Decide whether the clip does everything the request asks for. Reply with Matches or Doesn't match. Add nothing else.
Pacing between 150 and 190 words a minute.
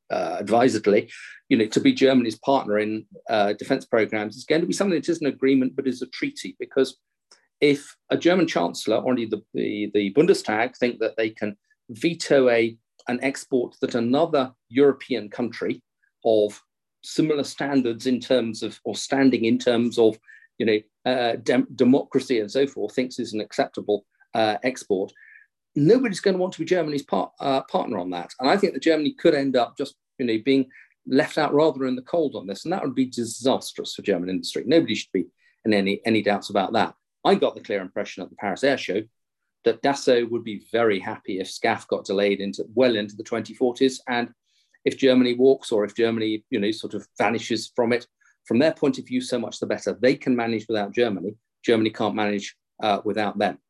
Doesn't match